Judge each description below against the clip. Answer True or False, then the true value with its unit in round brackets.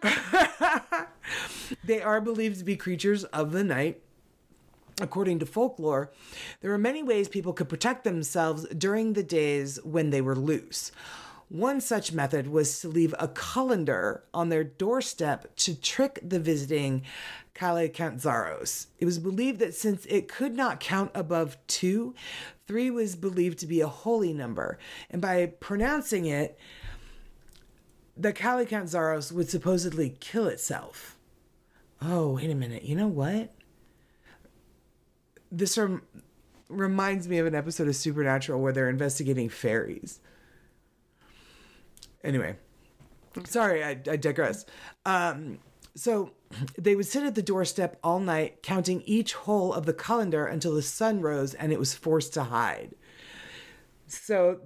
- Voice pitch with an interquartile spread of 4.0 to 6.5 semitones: True (5.2 semitones)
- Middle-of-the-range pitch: True (175 Hz)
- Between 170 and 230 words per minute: False (135 wpm)